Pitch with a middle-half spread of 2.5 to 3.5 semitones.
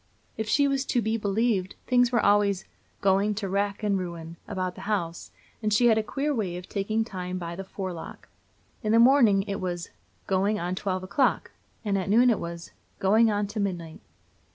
Yes: average, 3.0 semitones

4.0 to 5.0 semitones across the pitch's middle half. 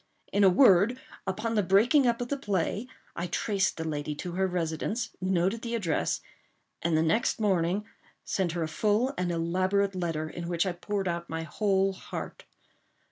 No: average, 3.6 semitones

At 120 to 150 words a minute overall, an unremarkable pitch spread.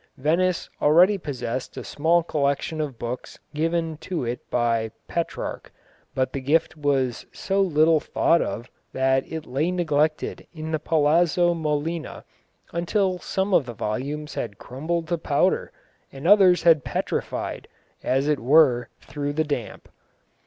Yes: average, 140 wpm; average, 4.0 semitones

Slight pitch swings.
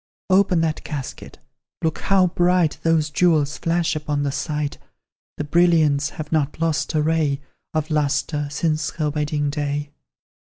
Yes: narrow, 2.0 semitones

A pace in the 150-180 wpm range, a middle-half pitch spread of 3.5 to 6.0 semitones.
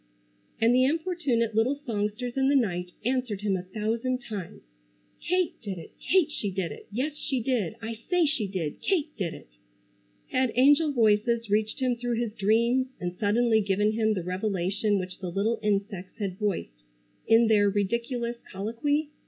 Yes: average, 170 wpm; average, 4.1 semitones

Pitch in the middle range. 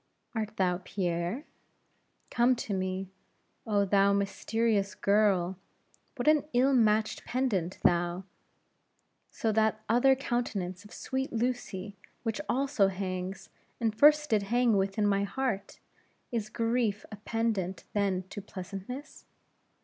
No: high, 210 Hz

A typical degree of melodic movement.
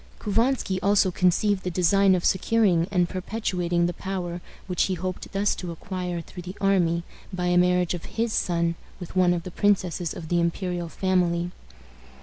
No: narrow, 1.8 semitones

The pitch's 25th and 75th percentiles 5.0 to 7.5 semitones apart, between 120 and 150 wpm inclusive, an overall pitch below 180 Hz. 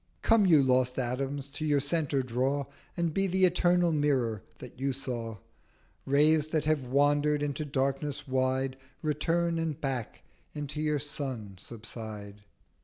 No: average, 2.9 semitones; average, 140 wpm; medium, 140 Hz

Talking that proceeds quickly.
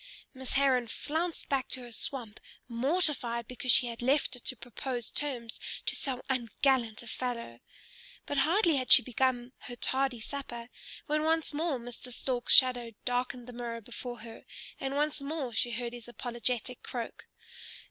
No: average, 160 wpm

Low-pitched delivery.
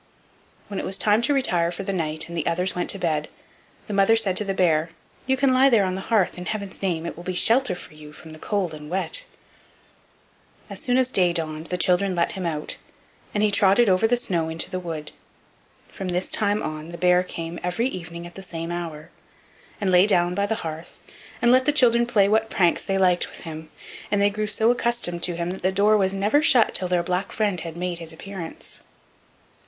No: medium, 185 Hz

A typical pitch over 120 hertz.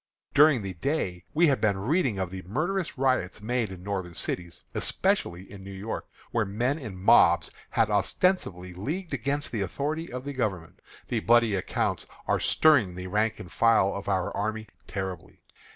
No: low, 105 Hz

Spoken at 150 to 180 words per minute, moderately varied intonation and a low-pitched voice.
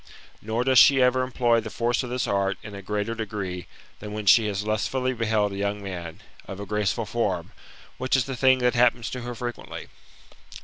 No: fast, 205 wpm; average, 3.3 semitones; low, 115 Hz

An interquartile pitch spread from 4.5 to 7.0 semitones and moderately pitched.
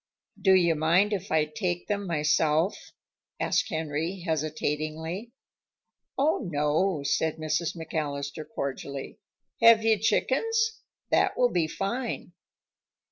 Yes: average, 4.8 semitones; medium, 165 Hz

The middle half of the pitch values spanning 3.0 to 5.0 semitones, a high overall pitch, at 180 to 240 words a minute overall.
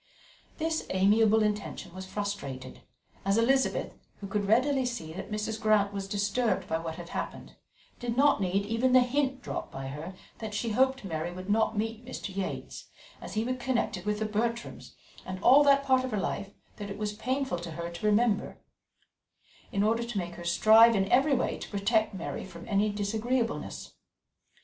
Yes: average, 3.8 semitones; high, 210 Hz; average, 185 wpm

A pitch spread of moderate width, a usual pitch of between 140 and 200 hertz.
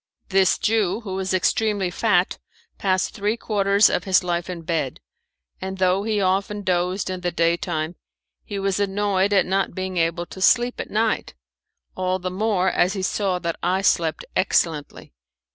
No: narrow, 2.1 semitones; high, 190 Hz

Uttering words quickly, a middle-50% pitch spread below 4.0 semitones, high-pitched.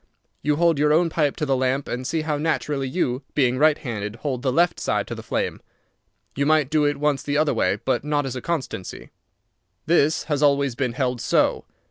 No: fast, 210 wpm; average, 2.9 semitones; medium, 145 Hz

